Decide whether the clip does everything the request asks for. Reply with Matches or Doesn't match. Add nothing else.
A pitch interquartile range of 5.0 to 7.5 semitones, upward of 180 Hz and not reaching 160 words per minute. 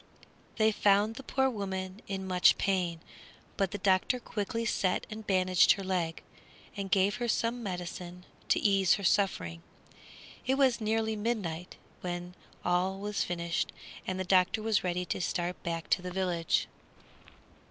Doesn't match